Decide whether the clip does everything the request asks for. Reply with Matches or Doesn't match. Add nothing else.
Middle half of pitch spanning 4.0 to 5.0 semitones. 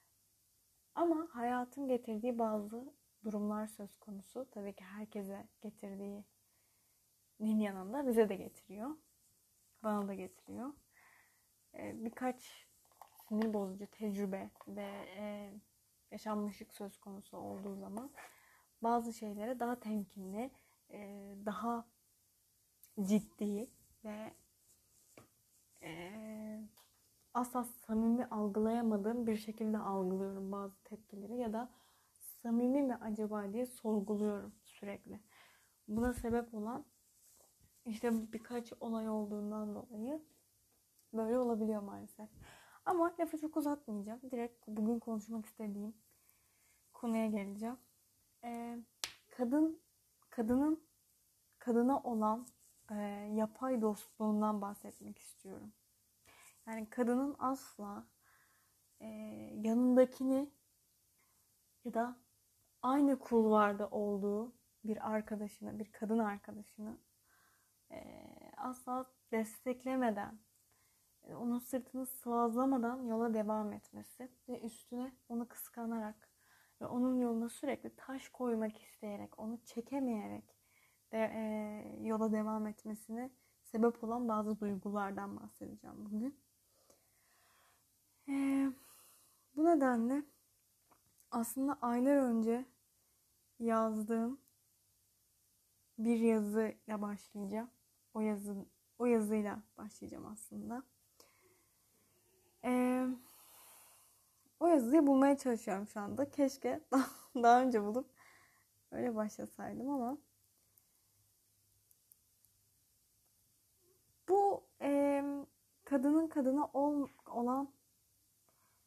Doesn't match